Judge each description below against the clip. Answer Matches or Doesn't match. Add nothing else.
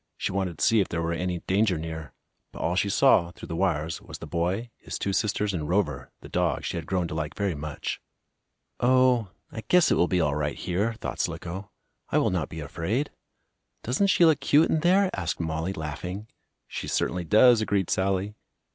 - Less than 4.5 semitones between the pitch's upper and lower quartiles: Doesn't match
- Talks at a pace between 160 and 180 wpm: Doesn't match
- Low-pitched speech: Matches